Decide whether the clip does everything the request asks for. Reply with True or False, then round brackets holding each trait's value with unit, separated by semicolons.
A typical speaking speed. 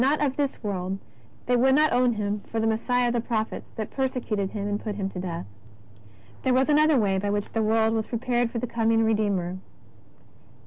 False (220 wpm)